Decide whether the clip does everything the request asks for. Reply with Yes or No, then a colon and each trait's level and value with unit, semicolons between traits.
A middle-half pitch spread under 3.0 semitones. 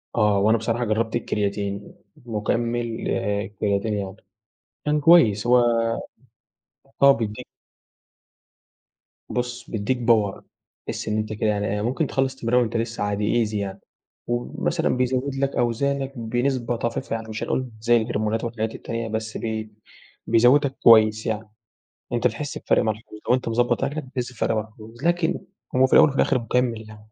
Yes: narrow, 2.5 semitones